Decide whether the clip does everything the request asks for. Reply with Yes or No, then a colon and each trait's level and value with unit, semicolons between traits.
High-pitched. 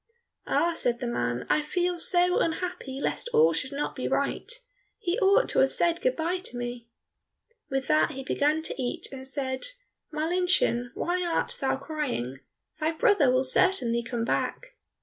Yes: very high, 300 Hz